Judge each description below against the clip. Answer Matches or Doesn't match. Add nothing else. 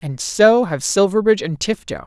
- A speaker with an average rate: Matches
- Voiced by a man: Doesn't match